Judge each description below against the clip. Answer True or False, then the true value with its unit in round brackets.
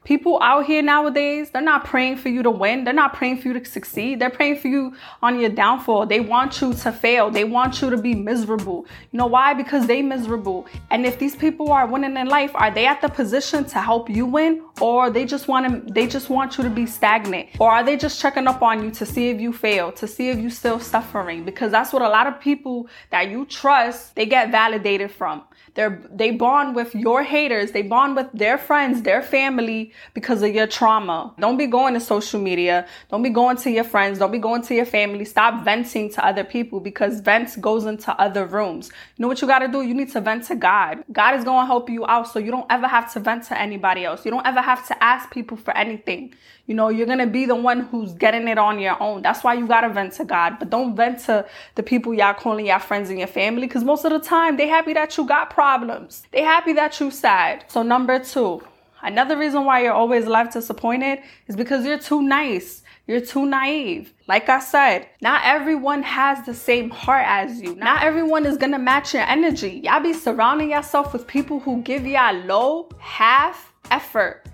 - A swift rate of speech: True (230 wpm)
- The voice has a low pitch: False (245 Hz)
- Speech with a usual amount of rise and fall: True (3.7 semitones)